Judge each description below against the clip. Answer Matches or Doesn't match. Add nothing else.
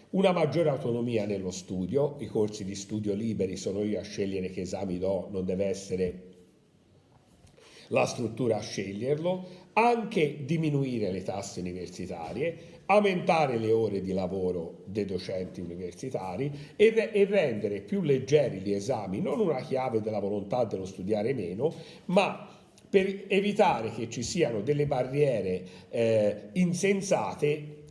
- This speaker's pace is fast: Doesn't match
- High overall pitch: Doesn't match